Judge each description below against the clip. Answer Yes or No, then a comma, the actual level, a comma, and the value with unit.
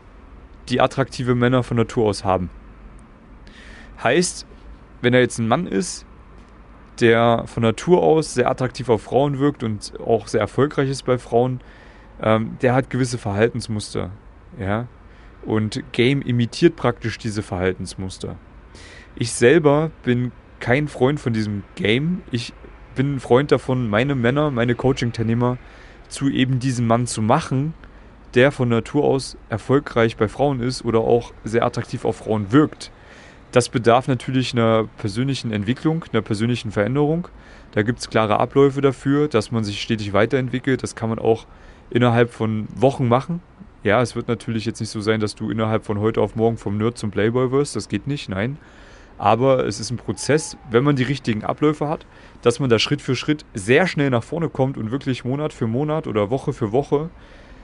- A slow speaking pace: No, average, 170 wpm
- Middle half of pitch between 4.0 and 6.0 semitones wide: No, average, 3.4 semitones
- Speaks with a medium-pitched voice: No, low, 120 Hz